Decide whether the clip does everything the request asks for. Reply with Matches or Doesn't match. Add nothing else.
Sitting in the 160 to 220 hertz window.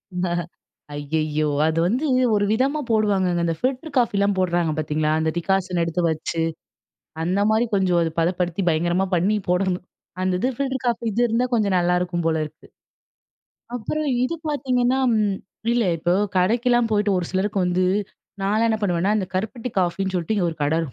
Matches